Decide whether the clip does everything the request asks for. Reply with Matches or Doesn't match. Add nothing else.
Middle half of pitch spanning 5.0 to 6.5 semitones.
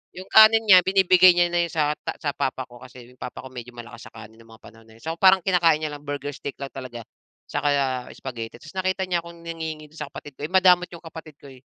Matches